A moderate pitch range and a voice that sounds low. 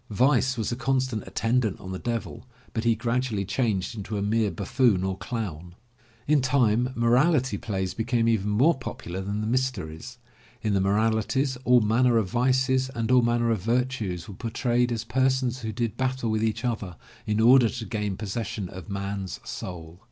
Yes: average, 3.7 semitones; low, 115 Hz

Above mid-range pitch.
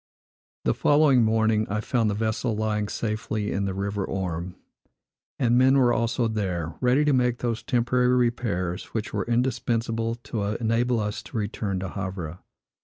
No: low, 110 Hz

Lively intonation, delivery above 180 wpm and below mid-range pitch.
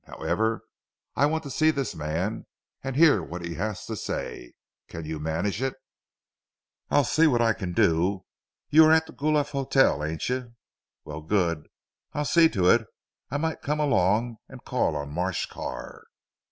No: wide, 9.0 semitones; average, 170 wpm; low, 115 Hz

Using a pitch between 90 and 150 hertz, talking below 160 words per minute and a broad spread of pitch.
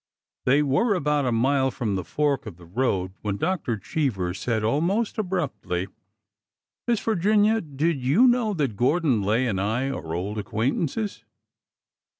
Yes: low, 135 Hz; average, 150 wpm; wide, 8.1 semitones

